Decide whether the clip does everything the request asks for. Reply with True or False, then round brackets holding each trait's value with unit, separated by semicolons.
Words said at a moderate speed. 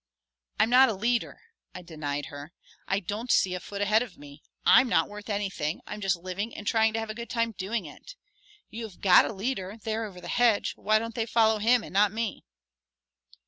False (215 wpm)